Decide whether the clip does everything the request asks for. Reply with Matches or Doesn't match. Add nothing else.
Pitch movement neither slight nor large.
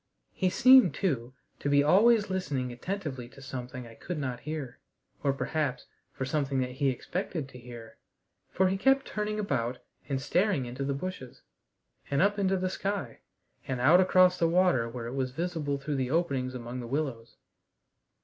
Doesn't match